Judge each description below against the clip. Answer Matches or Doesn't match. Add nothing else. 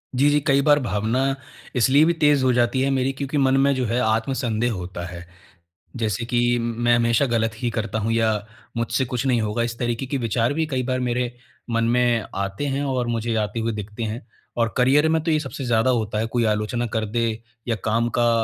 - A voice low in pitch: Matches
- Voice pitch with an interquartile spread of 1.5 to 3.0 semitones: Matches